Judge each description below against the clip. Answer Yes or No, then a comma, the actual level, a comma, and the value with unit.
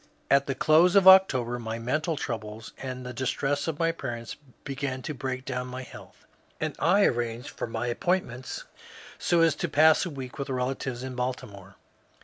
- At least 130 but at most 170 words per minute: No, average, 180 wpm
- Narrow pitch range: No, average, 4.0 semitones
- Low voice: Yes, low, 130 Hz